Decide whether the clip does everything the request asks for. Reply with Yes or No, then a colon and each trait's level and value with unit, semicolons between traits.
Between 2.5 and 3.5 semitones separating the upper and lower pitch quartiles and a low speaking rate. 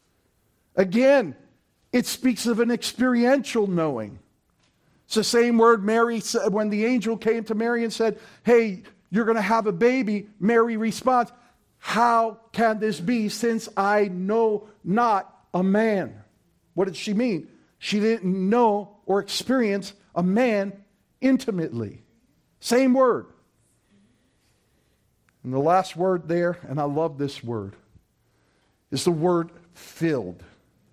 No: average, 4.7 semitones; slow, 130 wpm